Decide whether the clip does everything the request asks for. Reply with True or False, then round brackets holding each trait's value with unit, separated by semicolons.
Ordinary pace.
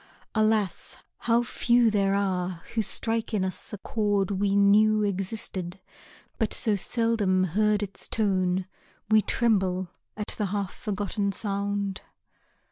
False (125 wpm)